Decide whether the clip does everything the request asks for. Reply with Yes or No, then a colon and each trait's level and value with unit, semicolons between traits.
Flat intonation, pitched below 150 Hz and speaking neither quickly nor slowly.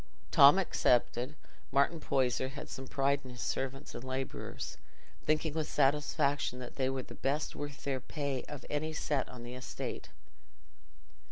Yes: narrow, 2.1 semitones; low, 135 Hz; average, 155 wpm